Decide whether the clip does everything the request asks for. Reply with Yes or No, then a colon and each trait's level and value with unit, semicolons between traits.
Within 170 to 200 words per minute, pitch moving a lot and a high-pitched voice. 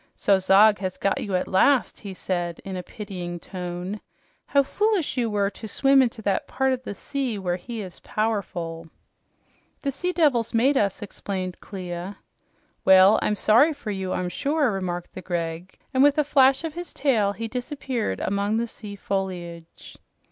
Yes: average, 175 wpm; wide, 5.9 semitones; high, 205 Hz